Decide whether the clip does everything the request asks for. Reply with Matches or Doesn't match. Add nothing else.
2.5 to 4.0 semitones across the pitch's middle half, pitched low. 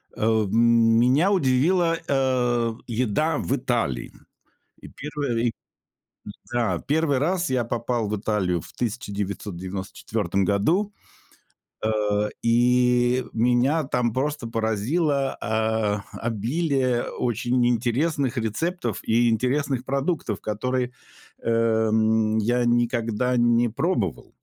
Matches